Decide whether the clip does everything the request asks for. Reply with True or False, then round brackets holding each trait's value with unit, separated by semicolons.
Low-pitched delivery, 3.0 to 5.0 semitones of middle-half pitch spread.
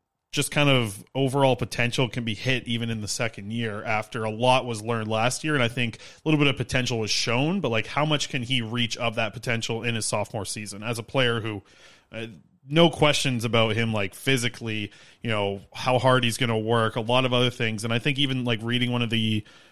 False (120 Hz; 2.6 semitones)